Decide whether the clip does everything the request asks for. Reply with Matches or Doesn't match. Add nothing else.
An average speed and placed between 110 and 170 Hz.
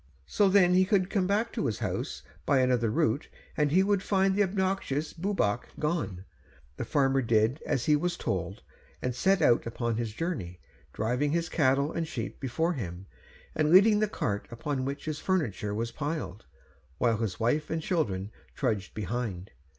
Matches